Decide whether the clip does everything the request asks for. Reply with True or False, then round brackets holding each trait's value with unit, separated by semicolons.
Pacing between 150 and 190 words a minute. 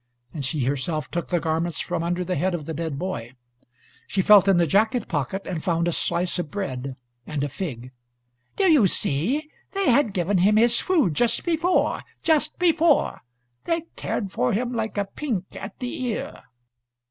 True (180 wpm)